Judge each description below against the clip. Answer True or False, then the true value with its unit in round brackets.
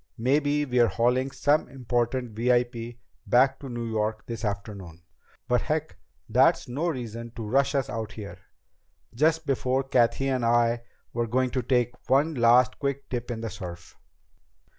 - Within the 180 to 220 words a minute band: False (155 wpm)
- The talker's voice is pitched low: True (120 Hz)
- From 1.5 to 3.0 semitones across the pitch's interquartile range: True (2.6 semitones)